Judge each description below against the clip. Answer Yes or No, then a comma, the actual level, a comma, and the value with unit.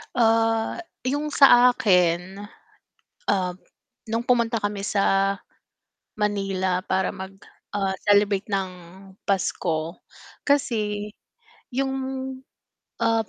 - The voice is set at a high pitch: Yes, high, 205 Hz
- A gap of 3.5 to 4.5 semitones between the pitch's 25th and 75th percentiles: No, average, 3.1 semitones